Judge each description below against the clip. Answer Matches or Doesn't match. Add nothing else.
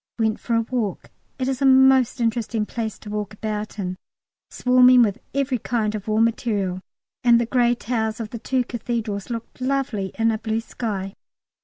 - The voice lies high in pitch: Matches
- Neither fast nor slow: Matches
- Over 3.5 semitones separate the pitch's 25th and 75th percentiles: Doesn't match